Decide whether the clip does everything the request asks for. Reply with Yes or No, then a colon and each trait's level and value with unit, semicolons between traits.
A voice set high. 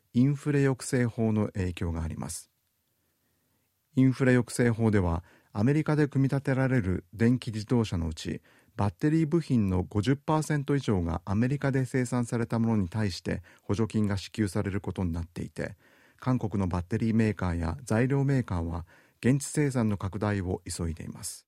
No: low, 110 Hz